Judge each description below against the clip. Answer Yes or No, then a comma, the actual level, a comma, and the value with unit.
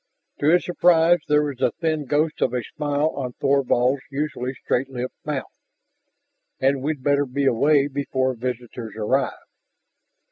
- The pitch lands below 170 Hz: Yes, medium, 140 Hz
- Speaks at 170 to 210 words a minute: No, average, 145 wpm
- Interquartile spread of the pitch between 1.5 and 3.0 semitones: Yes, average, 2.7 semitones